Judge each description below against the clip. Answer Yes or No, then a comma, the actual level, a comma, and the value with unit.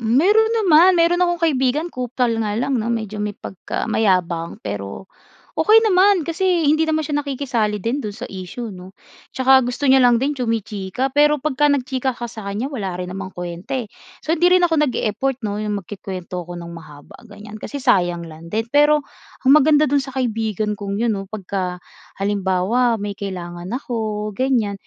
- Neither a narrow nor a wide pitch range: No, wide, 6.5 semitones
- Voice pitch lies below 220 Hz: No, high, 230 Hz